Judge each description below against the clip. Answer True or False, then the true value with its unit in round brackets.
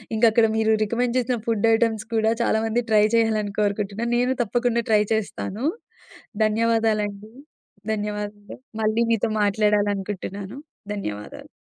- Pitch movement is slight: True (1.8 semitones)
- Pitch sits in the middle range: False (220 Hz)